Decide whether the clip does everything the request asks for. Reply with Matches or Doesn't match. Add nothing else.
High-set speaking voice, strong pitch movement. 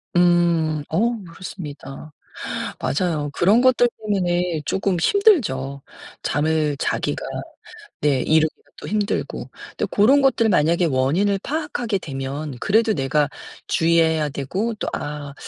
Doesn't match